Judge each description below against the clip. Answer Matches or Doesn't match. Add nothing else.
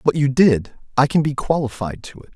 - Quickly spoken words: Matches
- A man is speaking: Matches